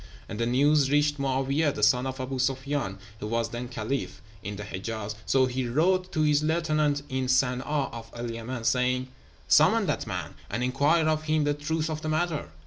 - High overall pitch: No, low, 135 Hz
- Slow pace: No, average, 195 wpm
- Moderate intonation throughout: Yes, average, 3.8 semitones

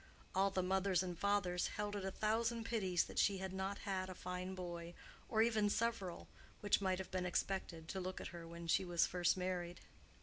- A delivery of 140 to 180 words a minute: No, average, 200 wpm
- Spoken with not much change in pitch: Yes, narrow, 2.2 semitones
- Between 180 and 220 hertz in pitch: Yes, high, 190 Hz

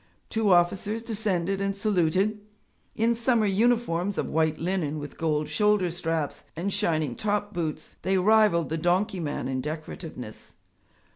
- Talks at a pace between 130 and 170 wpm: Yes, average, 140 wpm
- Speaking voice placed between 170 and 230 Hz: Yes, medium, 185 Hz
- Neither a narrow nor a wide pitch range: Yes, average, 4.5 semitones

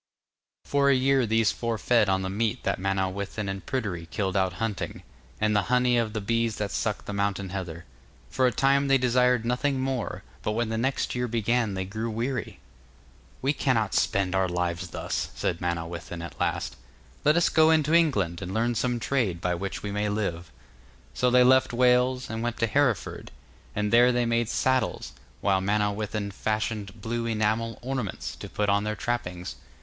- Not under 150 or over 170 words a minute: No, average, 185 wpm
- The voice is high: No, low, 110 Hz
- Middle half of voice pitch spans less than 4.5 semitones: Yes, average, 4.1 semitones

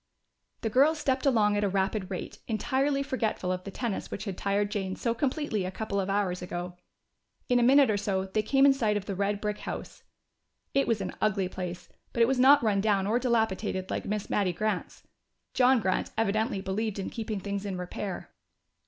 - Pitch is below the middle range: No, high, 210 Hz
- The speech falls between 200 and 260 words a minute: Yes, fast, 205 wpm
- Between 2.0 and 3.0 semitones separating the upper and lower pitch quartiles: No, average, 3.5 semitones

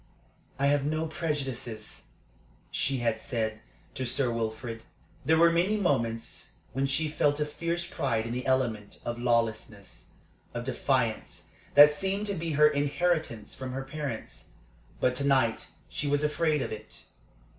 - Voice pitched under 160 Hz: Yes, low, 135 Hz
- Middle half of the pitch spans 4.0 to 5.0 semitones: Yes, average, 4.7 semitones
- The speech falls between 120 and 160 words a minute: Yes, average, 150 wpm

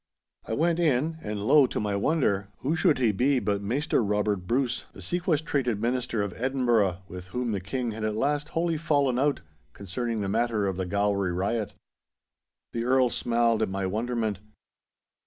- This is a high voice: No, low, 115 Hz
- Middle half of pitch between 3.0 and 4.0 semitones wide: No, average, 4.8 semitones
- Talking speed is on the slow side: No, average, 175 wpm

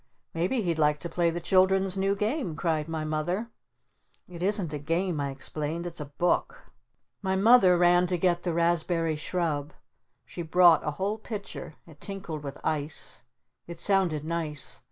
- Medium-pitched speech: Yes, medium, 170 Hz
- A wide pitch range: No, average, 3.4 semitones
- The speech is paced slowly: No, average, 165 wpm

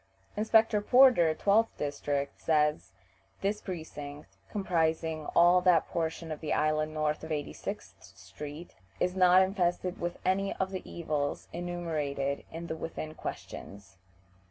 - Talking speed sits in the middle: No, slow, 130 wpm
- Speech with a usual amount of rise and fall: Yes, average, 3.4 semitones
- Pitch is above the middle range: No, medium, 165 Hz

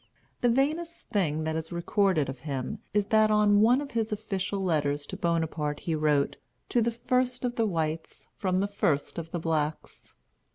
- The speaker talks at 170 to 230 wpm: Yes, average, 180 wpm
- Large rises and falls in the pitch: Yes, wide, 5.8 semitones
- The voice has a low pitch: No, medium, 185 Hz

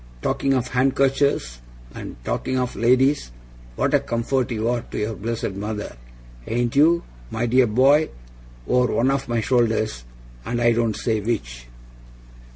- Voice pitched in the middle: No, low, 120 Hz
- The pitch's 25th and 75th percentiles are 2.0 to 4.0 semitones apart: Yes, average, 3.0 semitones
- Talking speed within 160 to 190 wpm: No, average, 150 wpm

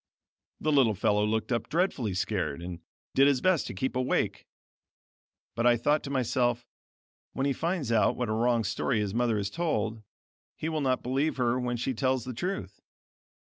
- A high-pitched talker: No, low, 125 Hz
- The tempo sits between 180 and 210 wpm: Yes, average, 185 wpm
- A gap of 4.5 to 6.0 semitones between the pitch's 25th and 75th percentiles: No, average, 3.8 semitones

